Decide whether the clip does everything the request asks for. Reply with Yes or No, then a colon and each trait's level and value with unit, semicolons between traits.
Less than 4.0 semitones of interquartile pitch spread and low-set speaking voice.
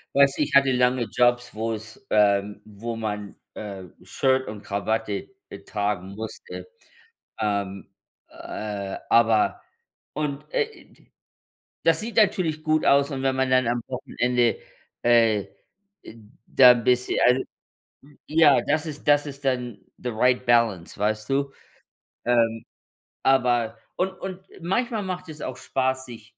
No: average, 4.4 semitones; low, 125 Hz